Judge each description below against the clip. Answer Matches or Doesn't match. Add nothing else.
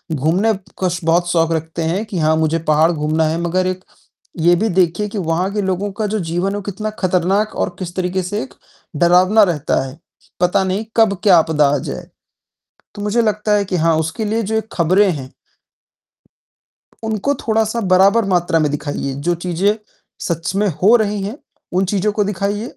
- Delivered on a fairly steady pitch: Doesn't match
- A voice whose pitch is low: Doesn't match